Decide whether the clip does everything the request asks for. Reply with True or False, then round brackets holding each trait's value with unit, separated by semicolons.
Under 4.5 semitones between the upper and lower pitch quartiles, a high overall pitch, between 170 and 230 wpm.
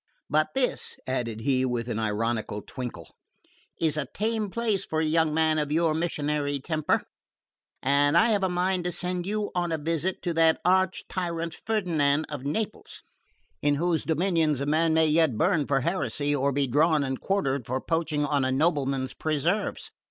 False (3.8 semitones; 155 Hz; 175 wpm)